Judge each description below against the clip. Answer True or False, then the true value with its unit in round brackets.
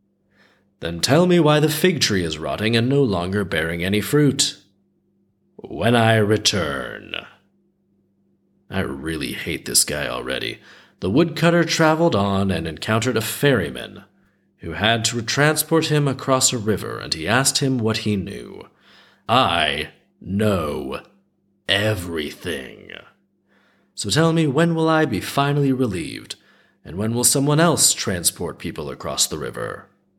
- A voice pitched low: True (115 Hz)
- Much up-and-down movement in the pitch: True (7.4 semitones)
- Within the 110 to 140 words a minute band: True (135 wpm)